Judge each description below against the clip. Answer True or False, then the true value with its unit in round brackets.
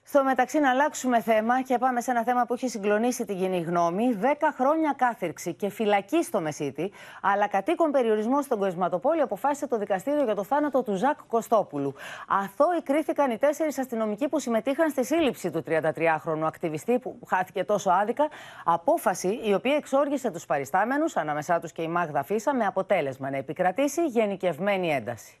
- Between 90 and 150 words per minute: False (170 wpm)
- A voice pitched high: True (225 Hz)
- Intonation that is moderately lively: False (7.3 semitones)